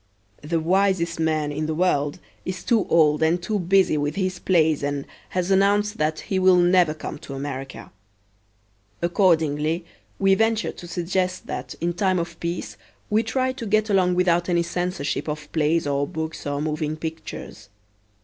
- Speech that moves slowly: No, average, 165 wpm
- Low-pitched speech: No, medium, 170 Hz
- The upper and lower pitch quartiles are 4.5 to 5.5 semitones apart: No, average, 3.5 semitones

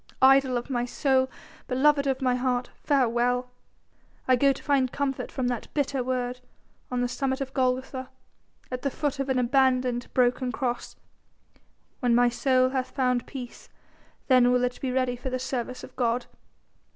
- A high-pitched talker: Yes, very high, 255 Hz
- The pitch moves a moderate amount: No, narrow, 1.3 semitones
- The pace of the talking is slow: No, average, 165 wpm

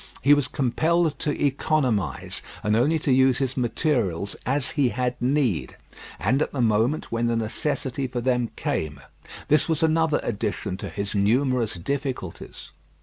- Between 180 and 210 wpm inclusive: No, average, 150 wpm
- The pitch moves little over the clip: No, average, 4.5 semitones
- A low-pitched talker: Yes, low, 130 Hz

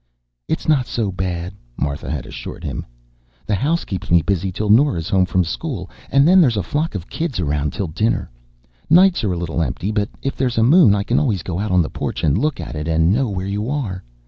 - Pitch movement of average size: No, wide, 6.9 semitones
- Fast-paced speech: Yes, fast, 230 wpm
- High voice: No, low, 100 Hz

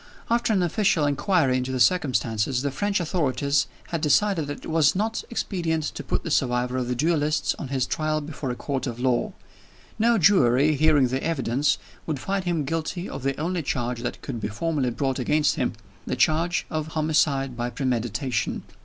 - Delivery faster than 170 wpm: Yes, average, 185 wpm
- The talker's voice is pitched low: No, medium, 145 Hz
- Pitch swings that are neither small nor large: Yes, average, 4.2 semitones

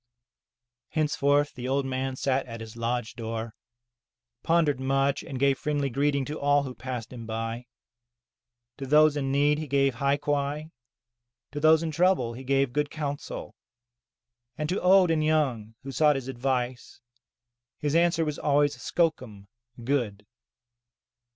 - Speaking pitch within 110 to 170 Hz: Yes, medium, 140 Hz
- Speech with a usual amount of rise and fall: Yes, average, 3.0 semitones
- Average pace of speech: Yes, average, 145 wpm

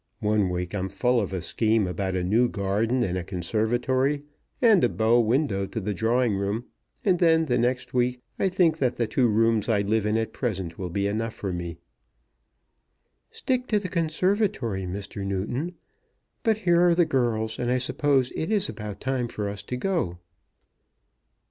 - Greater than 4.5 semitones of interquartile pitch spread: Yes, average, 5.1 semitones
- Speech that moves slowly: No, average, 180 wpm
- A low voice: Yes, low, 115 Hz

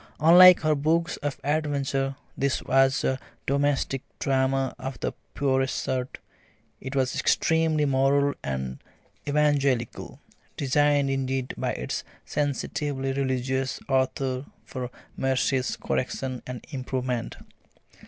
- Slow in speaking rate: Yes, slow, 105 wpm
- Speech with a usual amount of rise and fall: No, narrow, 1.6 semitones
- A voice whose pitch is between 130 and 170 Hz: Yes, low, 135 Hz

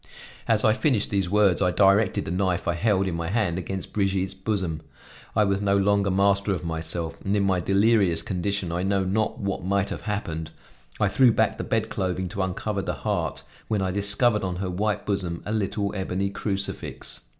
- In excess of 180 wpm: Yes, average, 195 wpm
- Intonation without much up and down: Yes, narrow, 2.0 semitones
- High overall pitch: No, low, 100 Hz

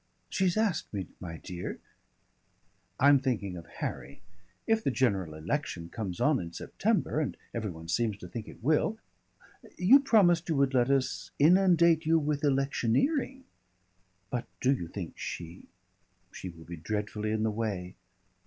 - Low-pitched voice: Yes, low, 120 Hz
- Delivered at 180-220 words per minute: No, average, 160 wpm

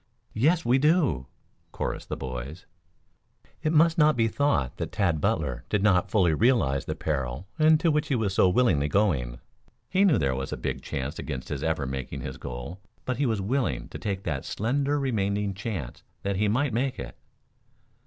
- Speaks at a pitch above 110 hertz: No, low, 100 Hz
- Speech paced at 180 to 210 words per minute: Yes, average, 185 wpm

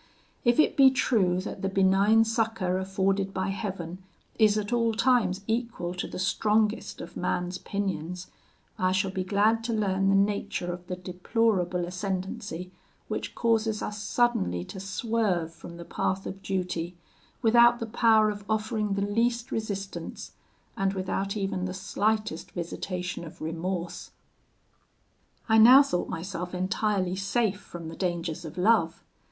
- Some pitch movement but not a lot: Yes, average, 3.2 semitones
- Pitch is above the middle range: Yes, high, 195 Hz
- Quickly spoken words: No, average, 145 wpm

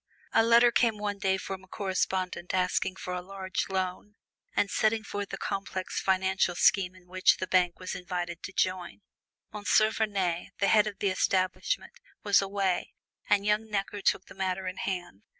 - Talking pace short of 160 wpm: No, average, 175 wpm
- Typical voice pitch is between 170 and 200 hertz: Yes, high, 190 Hz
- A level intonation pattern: Yes, narrow, 1.8 semitones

